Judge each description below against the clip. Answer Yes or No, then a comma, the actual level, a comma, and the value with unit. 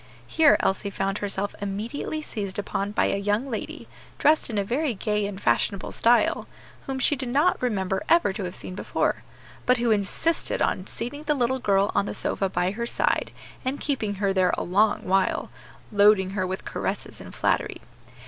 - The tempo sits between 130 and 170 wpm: No, average, 180 wpm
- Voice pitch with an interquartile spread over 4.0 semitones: Yes, average, 4.5 semitones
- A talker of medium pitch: No, high, 205 Hz